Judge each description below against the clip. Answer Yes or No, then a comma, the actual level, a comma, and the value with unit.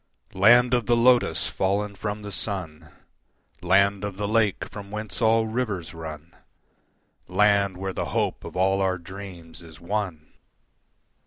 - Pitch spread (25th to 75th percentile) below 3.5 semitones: Yes, average, 2.7 semitones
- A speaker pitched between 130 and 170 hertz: No, low, 100 Hz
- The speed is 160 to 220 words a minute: No, average, 145 wpm